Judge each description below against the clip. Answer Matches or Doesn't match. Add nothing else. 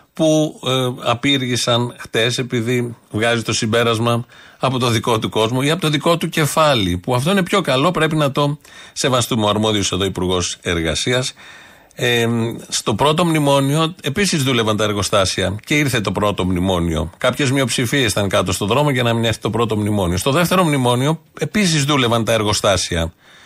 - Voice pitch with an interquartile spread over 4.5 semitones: Matches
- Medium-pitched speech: Doesn't match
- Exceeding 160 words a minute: Matches